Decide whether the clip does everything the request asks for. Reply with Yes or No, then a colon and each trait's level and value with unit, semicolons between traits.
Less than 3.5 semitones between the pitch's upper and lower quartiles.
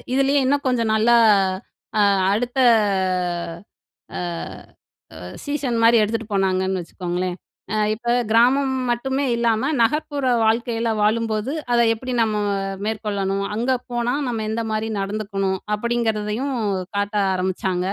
Yes: average, 2.7 semitones